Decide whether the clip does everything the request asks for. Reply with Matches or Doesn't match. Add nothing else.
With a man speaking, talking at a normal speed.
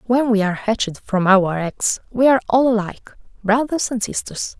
Doesn't match